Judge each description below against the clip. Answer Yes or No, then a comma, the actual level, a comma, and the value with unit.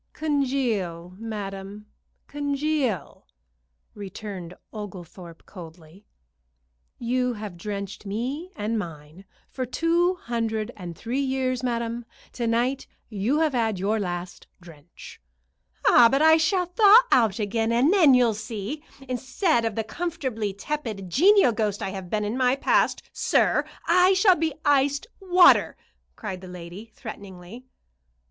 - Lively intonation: Yes, wide, 6.0 semitones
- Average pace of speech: No, slow, 130 wpm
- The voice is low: No, high, 230 Hz